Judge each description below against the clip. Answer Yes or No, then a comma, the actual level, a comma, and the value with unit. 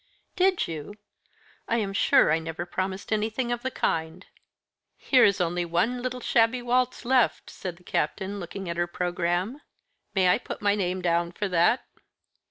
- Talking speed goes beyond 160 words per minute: Yes, average, 170 wpm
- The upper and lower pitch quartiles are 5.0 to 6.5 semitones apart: Yes, wide, 5.5 semitones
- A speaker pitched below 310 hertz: Yes, high, 190 Hz